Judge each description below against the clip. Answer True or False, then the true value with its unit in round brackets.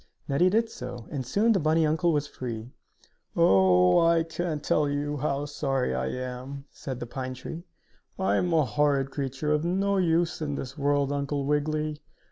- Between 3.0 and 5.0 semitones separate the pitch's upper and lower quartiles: True (3.5 semitones)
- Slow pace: False (175 wpm)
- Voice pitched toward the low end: False (145 Hz)